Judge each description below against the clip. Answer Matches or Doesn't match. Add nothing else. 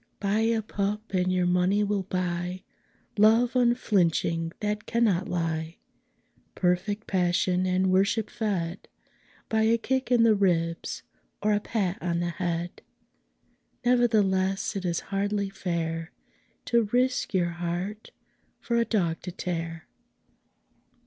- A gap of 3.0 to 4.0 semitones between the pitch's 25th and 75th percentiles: Matches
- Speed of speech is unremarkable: Doesn't match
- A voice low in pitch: Doesn't match